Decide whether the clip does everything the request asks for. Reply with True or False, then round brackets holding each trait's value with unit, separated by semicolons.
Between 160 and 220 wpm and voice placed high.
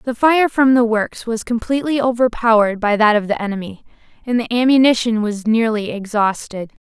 True (165 wpm; 230 Hz)